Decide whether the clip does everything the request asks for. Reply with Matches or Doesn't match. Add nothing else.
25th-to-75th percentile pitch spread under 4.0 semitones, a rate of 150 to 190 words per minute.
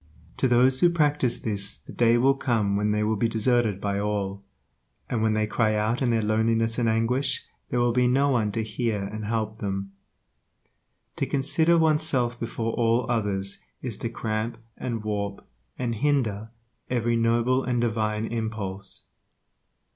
Matches